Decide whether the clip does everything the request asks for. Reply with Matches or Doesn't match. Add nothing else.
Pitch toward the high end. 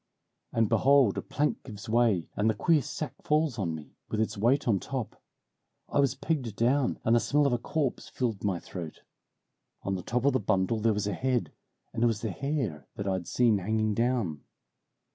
Doesn't match